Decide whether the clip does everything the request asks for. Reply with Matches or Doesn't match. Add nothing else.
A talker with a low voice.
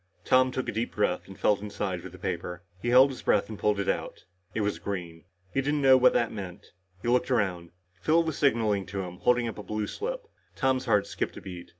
Matches